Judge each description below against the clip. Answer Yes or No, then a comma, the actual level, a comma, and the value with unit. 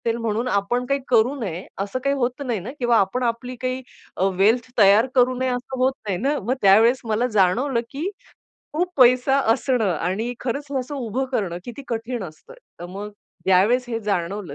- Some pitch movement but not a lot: Yes, average, 4.0 semitones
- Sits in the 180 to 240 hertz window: Yes, high, 235 Hz